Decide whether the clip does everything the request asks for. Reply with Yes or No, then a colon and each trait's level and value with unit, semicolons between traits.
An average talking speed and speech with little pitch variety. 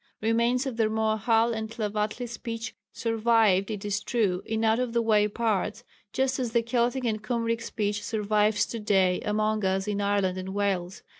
Yes: average, 175 wpm; narrow, 2.0 semitones